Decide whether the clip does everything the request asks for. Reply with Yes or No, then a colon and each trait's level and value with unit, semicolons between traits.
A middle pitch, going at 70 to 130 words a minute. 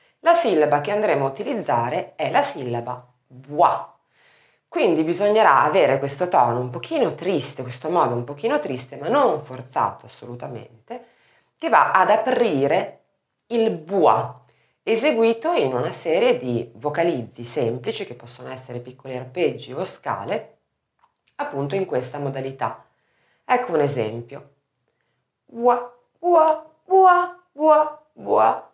Yes: medium, 150 Hz; average, 125 wpm